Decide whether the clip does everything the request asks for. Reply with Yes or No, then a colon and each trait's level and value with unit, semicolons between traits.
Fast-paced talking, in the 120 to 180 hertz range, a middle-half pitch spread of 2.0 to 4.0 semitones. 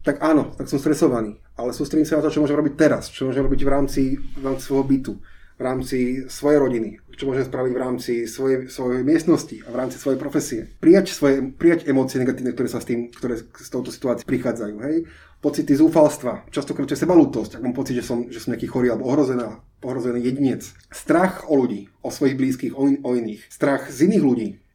Yes: fast, 210 wpm; low, 130 Hz; average, 2.8 semitones